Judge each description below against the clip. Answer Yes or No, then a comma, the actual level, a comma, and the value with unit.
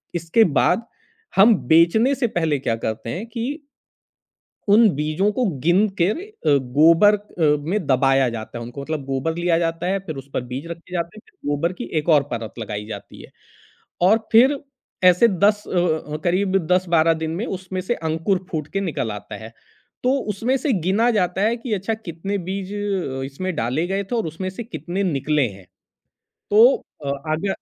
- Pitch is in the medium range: Yes, medium, 175 Hz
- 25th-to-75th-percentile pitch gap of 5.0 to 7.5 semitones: Yes, wide, 5.5 semitones